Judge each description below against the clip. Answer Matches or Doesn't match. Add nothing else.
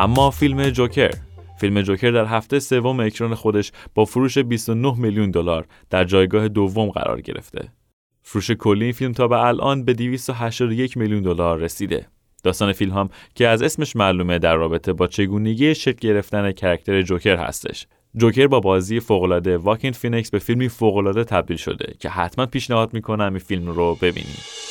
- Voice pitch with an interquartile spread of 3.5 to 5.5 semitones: Matches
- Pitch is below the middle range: Matches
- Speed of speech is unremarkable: Doesn't match